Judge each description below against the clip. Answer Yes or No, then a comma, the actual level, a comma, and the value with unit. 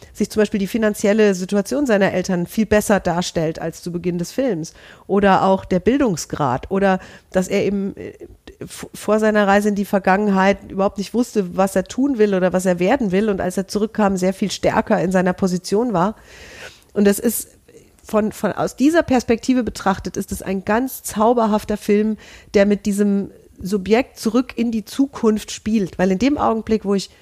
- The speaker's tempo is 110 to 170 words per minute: No, average, 185 wpm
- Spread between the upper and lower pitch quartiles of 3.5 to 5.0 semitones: No, narrow, 2.5 semitones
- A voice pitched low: No, high, 205 Hz